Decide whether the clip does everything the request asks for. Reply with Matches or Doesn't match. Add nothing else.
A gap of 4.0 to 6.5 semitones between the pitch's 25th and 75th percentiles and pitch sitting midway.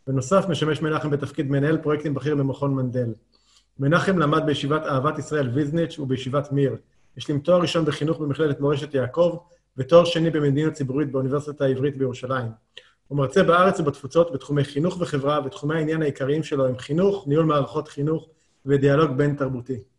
Doesn't match